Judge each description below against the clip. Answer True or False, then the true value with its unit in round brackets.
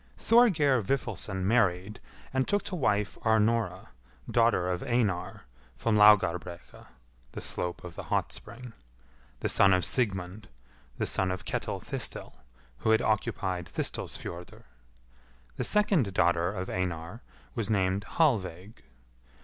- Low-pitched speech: True (105 Hz)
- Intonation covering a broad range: False (4.2 semitones)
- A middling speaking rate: False (125 wpm)